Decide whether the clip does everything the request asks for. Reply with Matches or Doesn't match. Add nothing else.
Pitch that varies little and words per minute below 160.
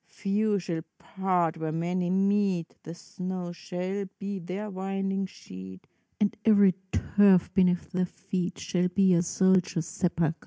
Matches